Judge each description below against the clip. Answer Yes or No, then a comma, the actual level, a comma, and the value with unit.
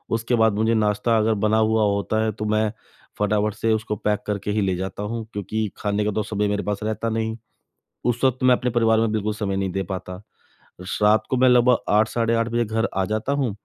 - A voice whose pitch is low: Yes, low, 110 Hz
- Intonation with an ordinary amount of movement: No, narrow, 1.6 semitones